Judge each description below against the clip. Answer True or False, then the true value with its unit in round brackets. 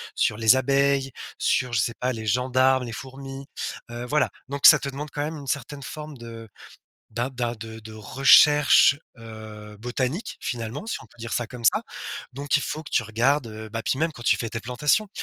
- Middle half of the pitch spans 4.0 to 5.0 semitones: False (3.4 semitones)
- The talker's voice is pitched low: True (125 Hz)